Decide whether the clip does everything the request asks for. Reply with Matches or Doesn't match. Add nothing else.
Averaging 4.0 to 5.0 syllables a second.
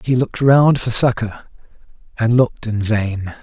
Matches